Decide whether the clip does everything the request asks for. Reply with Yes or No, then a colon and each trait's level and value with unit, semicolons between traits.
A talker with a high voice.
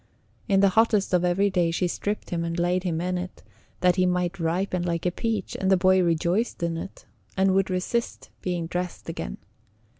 No: medium, 180 Hz